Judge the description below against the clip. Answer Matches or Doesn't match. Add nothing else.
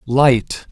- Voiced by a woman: Doesn't match